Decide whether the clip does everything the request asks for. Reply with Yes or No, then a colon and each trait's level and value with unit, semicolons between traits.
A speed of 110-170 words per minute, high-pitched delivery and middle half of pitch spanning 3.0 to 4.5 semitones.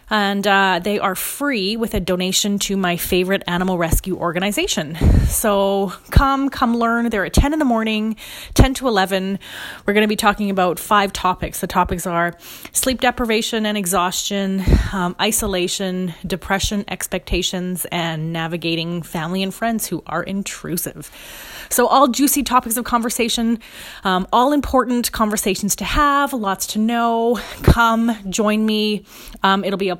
Yes: average, 150 wpm; high, 200 Hz; average, 3.8 semitones